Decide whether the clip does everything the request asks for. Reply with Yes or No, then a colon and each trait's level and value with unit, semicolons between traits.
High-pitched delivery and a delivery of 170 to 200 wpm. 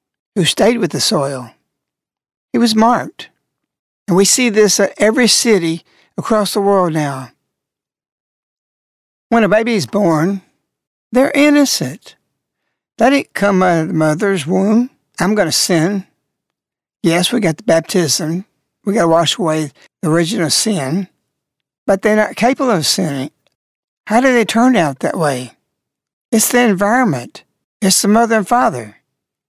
No: high, 200 Hz; average, 145 wpm